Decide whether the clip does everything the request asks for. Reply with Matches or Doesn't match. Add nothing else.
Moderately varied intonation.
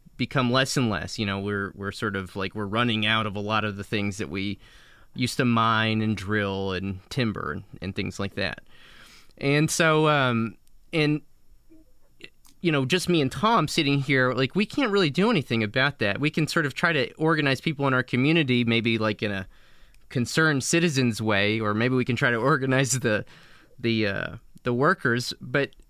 Doesn't match